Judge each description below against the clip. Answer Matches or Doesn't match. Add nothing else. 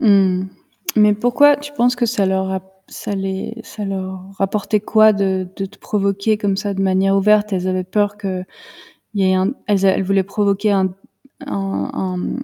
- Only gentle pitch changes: Matches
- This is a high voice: Matches